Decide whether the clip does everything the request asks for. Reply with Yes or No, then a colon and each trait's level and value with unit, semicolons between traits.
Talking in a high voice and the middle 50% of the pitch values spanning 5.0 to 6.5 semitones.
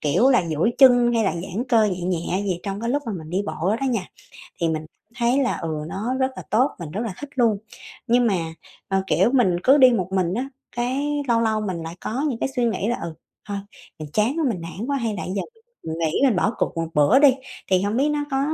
Yes: high, 220 Hz; wide, 5.5 semitones